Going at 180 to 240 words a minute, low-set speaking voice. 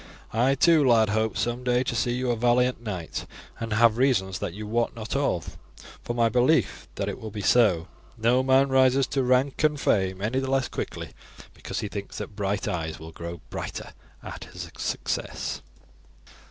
Yes: average, 185 wpm; low, 120 Hz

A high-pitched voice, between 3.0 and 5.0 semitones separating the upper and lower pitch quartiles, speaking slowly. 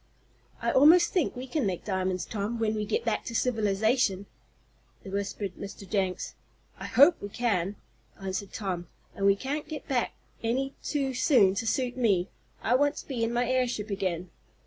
No: high, 220 Hz; average, 4.7 semitones; average, 170 wpm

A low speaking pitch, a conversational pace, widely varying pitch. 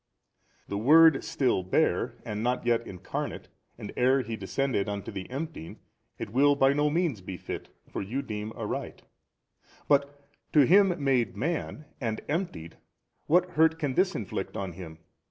Yes: low, 130 Hz; average, 155 wpm; wide, 6.2 semitones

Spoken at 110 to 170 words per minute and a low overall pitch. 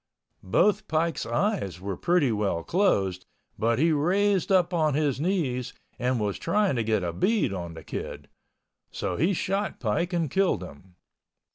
No: average, 155 wpm; medium, 150 Hz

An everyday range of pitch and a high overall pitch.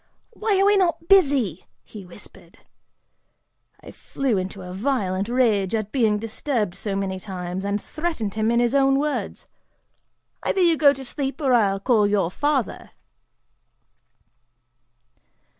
No: wide, 6.1 semitones; high, 225 Hz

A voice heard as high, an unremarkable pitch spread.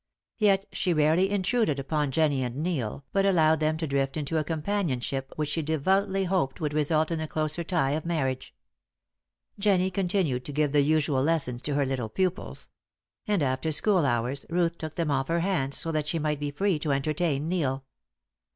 No: medium, 155 Hz; average, 3.8 semitones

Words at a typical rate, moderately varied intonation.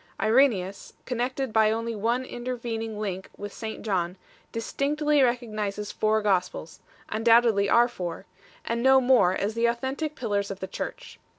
Yes: average, 150 wpm; average, 3.5 semitones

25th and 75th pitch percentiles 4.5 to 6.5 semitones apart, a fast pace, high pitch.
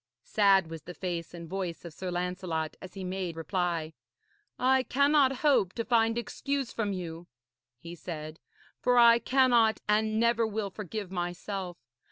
No: average, 4.9 semitones; average, 155 wpm; high, 195 Hz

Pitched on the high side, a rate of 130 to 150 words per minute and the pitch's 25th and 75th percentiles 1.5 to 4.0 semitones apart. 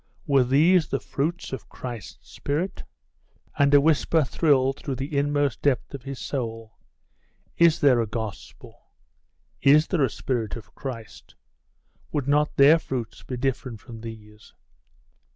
No: low, 135 Hz; average, 140 wpm; average, 3.5 semitones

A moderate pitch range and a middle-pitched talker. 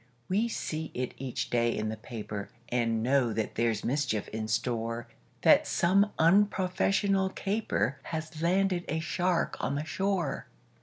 No: wide, 8.1 semitones; medium, 145 Hz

